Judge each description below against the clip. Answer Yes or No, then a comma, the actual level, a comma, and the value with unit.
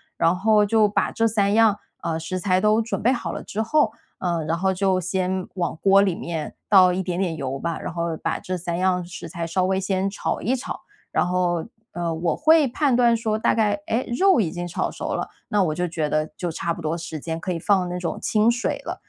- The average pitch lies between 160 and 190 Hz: Yes, medium, 185 Hz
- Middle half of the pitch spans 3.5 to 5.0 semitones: Yes, average, 3.8 semitones